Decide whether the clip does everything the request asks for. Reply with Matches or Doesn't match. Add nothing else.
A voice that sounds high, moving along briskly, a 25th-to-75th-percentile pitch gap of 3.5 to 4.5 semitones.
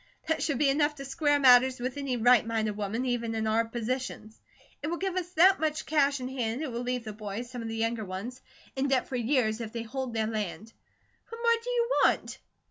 Matches